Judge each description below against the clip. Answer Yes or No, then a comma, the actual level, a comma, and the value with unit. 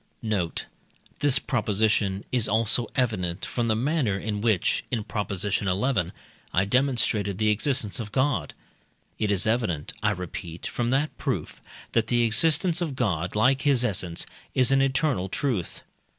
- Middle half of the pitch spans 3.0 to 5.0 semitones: Yes, average, 4.6 semitones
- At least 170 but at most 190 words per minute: No, average, 150 wpm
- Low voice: Yes, low, 110 Hz